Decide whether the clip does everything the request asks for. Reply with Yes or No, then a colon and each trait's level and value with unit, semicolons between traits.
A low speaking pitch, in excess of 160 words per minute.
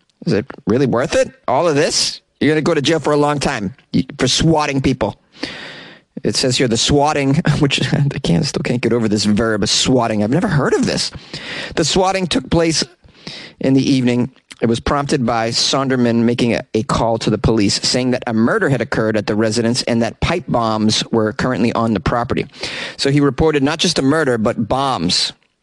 Yes: low, 130 Hz; fast, 205 wpm